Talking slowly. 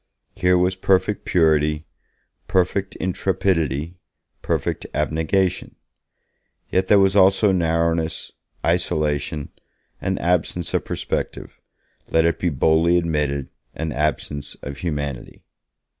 Yes: slow, 100 wpm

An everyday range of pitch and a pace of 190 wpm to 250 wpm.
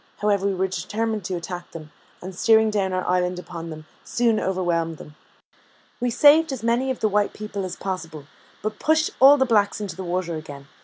Yes: average, 4.1 semitones; average, 200 wpm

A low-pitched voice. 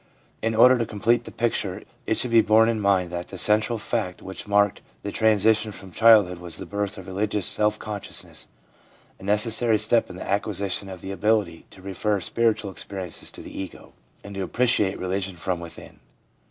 Yes: low, 100 Hz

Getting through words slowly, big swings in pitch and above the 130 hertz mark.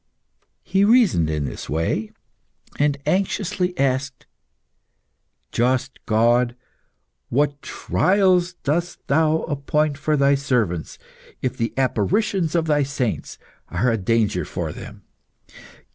Yes: slow, 110 wpm; wide, 6.0 semitones; medium, 140 Hz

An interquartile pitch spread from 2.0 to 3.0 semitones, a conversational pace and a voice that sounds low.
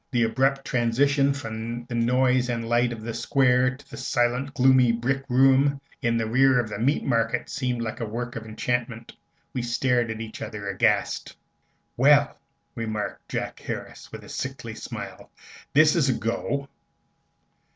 Yes: narrow, 2.5 semitones; average, 160 wpm; low, 120 Hz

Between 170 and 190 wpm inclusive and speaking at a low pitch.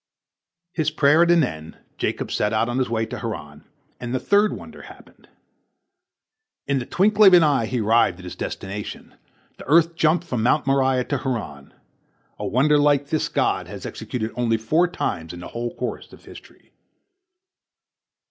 Yes: average, 175 wpm; low, 130 Hz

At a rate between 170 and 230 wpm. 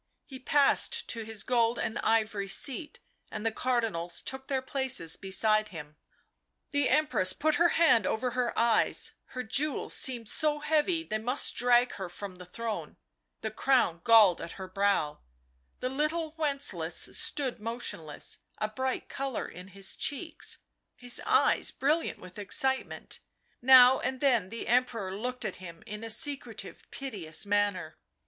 No: average, 150 wpm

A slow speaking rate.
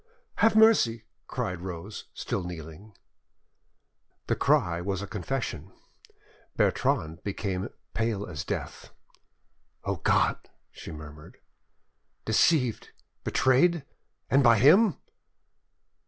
Yes: slow, 90 wpm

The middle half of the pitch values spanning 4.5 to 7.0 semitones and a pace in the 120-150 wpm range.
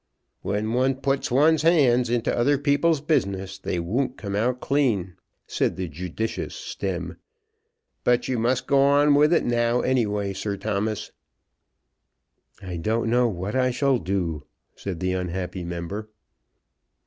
Yes: wide, 5.6 semitones; average, 145 wpm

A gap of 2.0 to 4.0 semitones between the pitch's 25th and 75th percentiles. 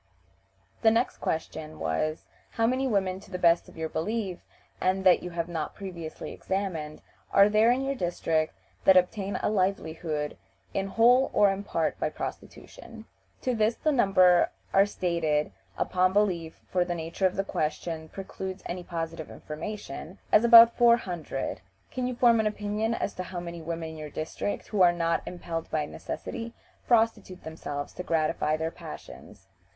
No: average, 4.5 semitones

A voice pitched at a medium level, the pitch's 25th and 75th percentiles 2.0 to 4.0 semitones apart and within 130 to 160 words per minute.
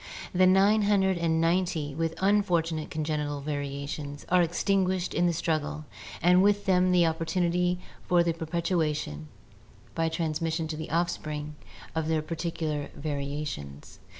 Yes: medium, 165 Hz; average, 2.8 semitones; average, 140 wpm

